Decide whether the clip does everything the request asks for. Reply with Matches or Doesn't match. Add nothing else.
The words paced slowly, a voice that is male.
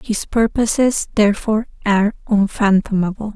Doesn't match